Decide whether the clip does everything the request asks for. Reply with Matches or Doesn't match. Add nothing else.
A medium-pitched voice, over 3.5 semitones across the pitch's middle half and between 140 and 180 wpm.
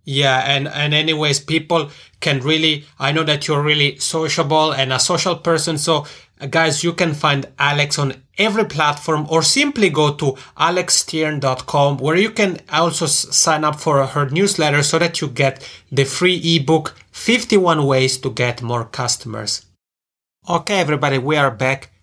Doesn't match